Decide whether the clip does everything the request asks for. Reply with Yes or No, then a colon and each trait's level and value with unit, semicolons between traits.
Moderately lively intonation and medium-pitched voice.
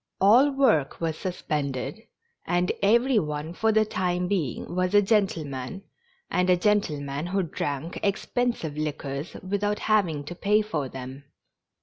No: wide, 5.7 semitones; medium, 180 Hz